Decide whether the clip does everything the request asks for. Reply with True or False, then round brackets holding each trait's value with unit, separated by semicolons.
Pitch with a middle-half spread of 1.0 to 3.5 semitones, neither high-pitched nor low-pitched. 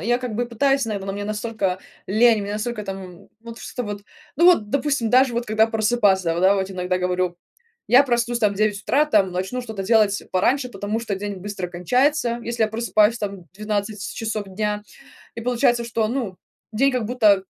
False (3.1 semitones; 215 Hz)